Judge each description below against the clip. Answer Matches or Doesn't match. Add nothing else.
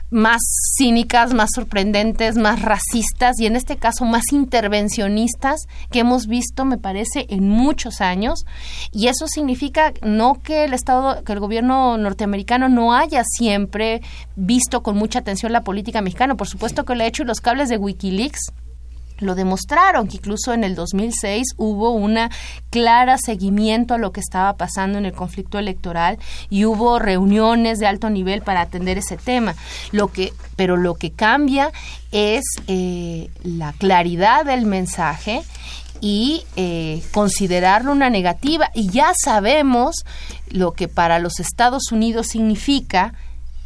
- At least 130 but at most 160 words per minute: Matches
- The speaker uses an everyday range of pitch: Matches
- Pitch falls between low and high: Doesn't match